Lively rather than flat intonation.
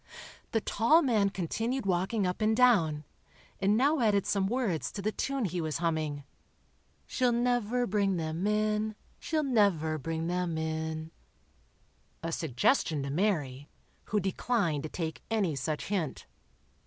Yes: wide, 5.7 semitones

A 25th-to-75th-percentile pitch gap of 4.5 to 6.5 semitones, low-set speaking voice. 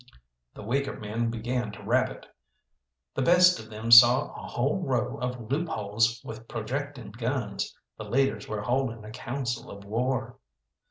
No: average, 3.2 semitones; low, 120 Hz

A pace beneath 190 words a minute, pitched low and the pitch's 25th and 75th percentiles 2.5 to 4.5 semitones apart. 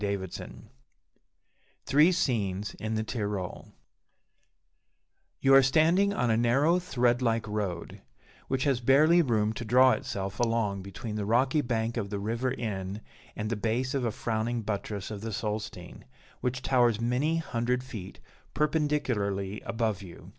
Yes: average, 145 wpm; low, 115 Hz; average, 3.9 semitones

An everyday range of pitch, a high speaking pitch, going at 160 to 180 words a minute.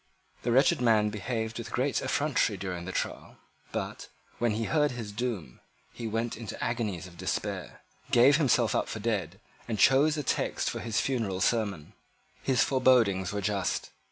No: average, 3.8 semitones; low, 115 Hz; average, 165 wpm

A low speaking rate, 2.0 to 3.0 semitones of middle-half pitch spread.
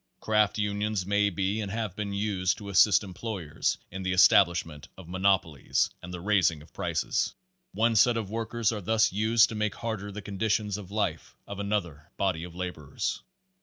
No: average, 175 wpm; average, 2.7 semitones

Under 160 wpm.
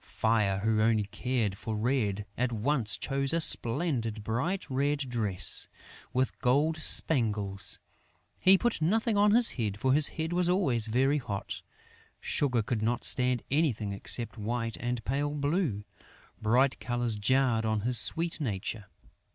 Yes: average, 145 wpm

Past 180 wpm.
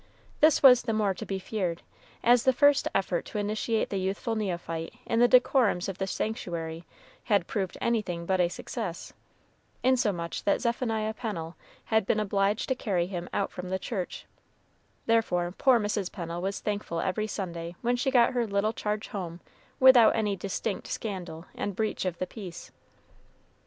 No: average, 165 wpm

